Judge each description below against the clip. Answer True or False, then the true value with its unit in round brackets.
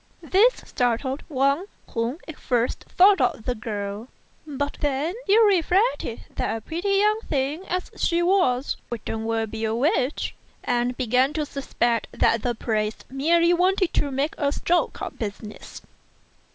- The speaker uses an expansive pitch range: True (6.6 semitones)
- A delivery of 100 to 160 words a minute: True (150 wpm)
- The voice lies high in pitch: True (275 Hz)